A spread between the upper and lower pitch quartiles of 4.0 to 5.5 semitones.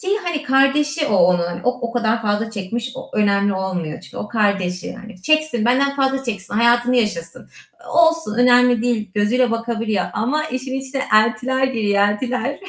Yes: average, 4.3 semitones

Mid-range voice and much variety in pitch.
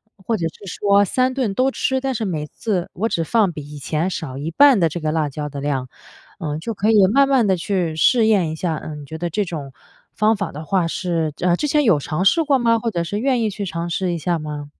Yes: medium, 180 Hz; wide, 5.9 semitones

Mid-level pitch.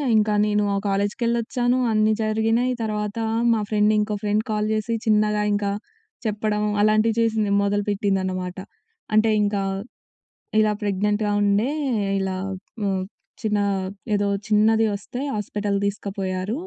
No: high, 210 Hz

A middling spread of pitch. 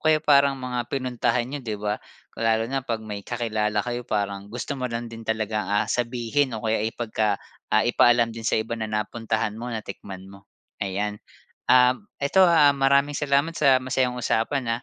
Yes: average, 3.1 semitones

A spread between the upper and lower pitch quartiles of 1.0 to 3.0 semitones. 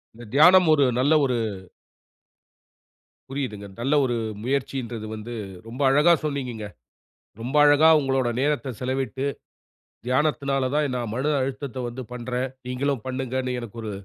Yes: narrow, 2.5 semitones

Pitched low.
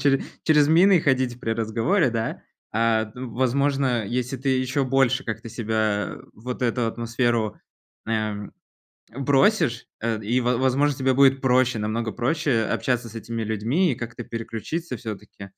Yes: low, 120 Hz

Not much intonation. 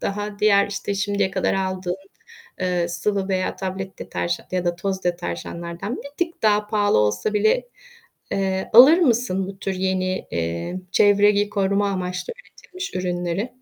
Yes: narrow, 2.2 semitones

